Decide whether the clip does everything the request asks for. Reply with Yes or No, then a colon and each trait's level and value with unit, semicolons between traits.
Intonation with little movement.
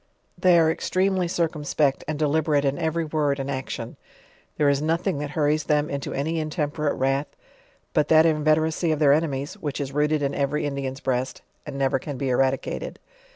Yes: narrow, 2.3 semitones